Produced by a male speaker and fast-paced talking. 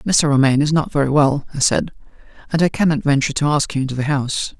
Yes: male; fast, 235 wpm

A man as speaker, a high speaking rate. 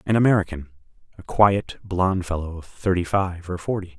No: male; average, 150 wpm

